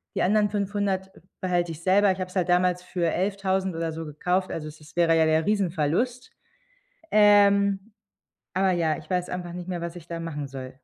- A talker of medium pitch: Yes, medium, 180 Hz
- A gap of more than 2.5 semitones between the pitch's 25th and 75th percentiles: Yes, average, 2.9 semitones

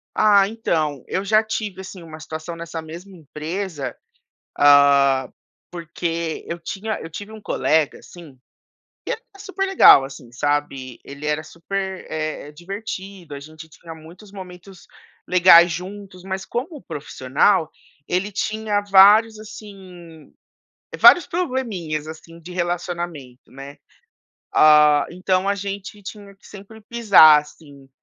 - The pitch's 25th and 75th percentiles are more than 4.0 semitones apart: Yes, average, 4.6 semitones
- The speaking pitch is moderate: Yes, medium, 175 Hz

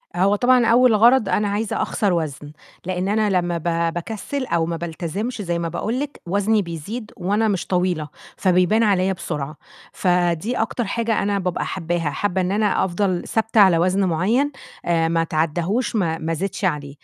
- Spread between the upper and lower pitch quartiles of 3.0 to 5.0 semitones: Yes, average, 4.2 semitones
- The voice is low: No, medium, 185 Hz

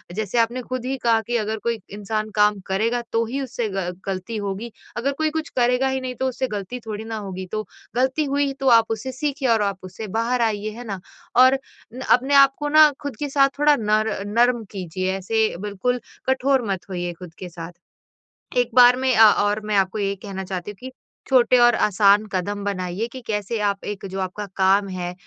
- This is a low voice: No, high, 220 Hz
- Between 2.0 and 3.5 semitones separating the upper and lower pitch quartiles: No, average, 4.2 semitones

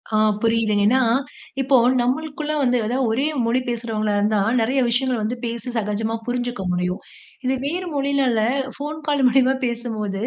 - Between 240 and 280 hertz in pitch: Yes, high, 245 Hz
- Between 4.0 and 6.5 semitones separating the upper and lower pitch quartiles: No, average, 3.5 semitones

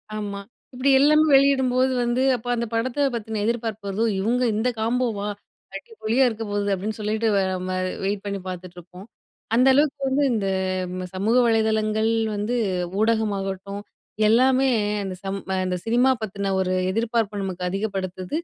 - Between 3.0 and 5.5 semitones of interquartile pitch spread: Yes, average, 3.7 semitones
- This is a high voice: Yes, high, 220 Hz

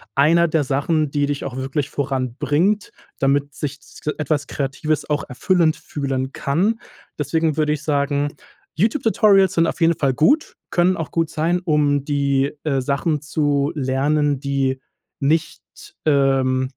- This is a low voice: No, medium, 145 Hz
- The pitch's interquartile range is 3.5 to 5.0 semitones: No, average, 2.7 semitones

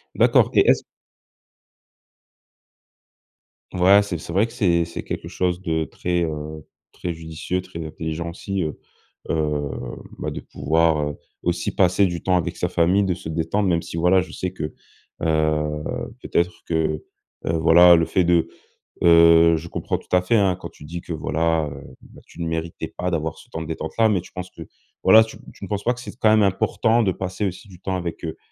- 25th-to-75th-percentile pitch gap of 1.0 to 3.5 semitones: Yes, narrow, 2.5 semitones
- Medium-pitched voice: No, very low, 85 Hz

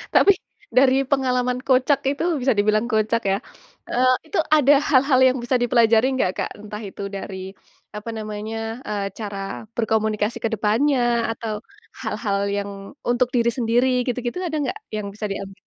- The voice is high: Yes, high, 230 Hz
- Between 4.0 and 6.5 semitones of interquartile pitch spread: No, average, 3.3 semitones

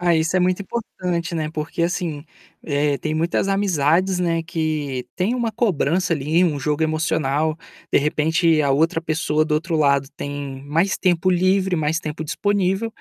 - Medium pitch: Yes, medium, 165 Hz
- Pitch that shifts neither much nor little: Yes, average, 3.1 semitones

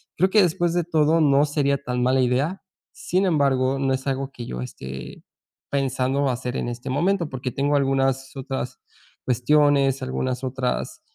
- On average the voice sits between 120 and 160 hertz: Yes, low, 135 Hz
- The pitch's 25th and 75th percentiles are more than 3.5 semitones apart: No, narrow, 2.4 semitones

